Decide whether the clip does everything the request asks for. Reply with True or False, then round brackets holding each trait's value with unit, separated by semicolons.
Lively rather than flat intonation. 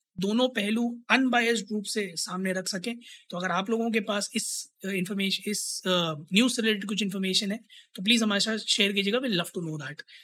False (3.1 semitones)